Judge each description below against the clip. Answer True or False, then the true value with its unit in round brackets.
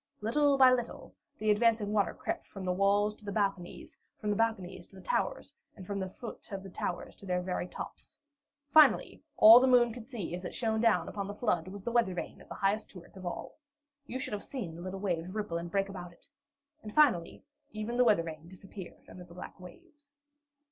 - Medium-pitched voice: False (200 Hz)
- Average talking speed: False (215 wpm)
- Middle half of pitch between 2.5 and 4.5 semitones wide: True (4.0 semitones)